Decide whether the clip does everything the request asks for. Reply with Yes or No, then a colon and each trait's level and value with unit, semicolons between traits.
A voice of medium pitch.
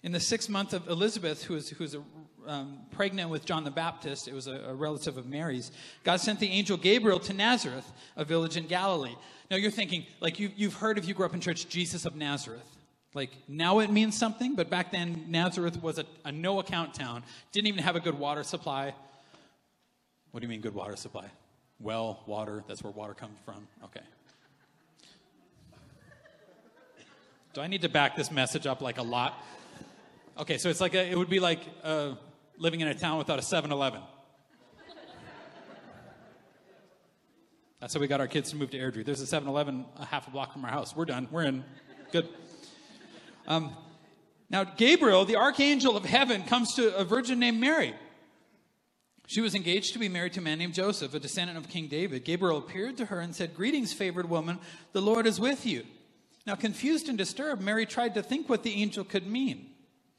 Yes: medium, 165 Hz